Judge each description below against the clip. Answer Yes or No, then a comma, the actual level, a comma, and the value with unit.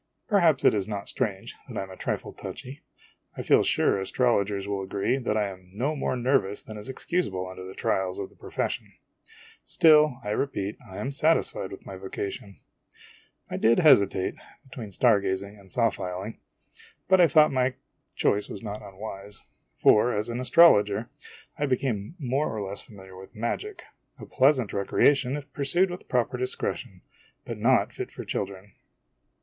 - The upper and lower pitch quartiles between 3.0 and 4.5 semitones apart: No, wide, 5.4 semitones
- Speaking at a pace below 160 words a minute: No, average, 170 wpm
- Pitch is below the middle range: Yes, low, 110 Hz